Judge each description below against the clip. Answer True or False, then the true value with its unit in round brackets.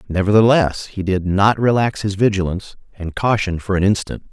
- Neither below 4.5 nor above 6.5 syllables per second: True (5.3 syllables/s)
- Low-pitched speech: True (100 Hz)